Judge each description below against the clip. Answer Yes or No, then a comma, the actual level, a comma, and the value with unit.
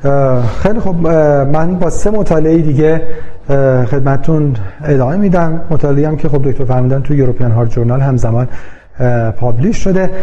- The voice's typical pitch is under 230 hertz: Yes, medium, 140 Hz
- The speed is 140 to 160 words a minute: No, average, 130 wpm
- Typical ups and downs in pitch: Yes, average, 4.2 semitones